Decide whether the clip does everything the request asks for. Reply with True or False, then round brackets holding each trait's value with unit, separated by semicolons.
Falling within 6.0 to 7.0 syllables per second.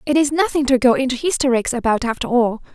True (6.3 syllables/s)